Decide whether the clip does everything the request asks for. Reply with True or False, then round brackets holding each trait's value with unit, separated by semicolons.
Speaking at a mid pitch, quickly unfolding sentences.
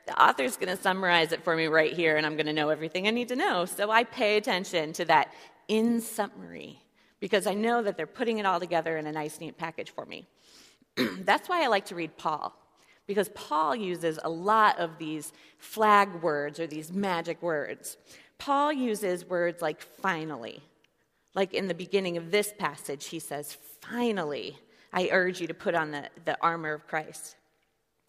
False (175 Hz; 190 wpm)